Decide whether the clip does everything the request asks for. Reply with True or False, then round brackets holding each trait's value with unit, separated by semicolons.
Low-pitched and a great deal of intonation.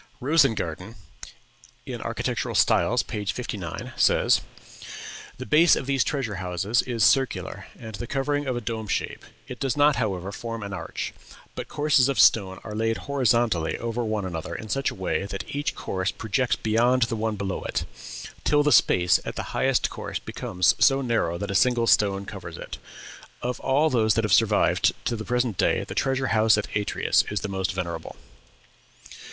False (115 Hz; 4.6 semitones)